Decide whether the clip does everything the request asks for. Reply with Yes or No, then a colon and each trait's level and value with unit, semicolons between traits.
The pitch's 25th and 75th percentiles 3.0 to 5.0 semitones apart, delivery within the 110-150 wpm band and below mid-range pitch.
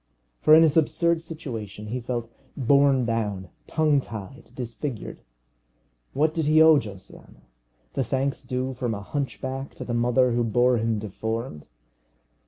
Yes: average, 3.8 semitones; average, 145 wpm; low, 125 Hz